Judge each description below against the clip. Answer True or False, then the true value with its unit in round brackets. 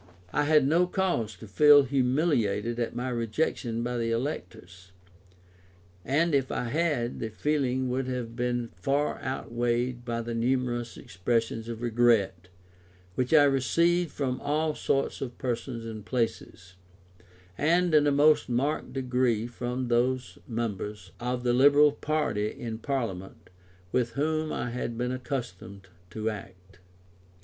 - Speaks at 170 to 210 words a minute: False (140 wpm)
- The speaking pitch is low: True (125 Hz)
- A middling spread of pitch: True (3.4 semitones)